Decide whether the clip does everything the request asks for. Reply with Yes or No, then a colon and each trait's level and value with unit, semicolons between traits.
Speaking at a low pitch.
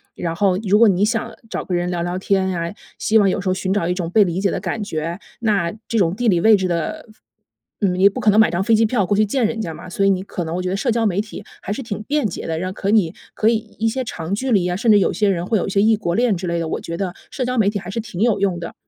No: high, 195 Hz